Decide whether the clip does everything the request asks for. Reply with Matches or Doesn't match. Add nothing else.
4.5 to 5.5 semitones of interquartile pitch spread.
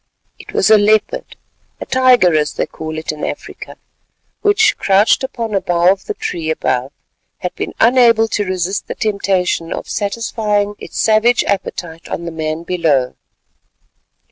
Matches